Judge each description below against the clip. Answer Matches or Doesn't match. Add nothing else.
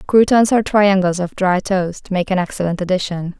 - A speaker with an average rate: Matches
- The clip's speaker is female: Matches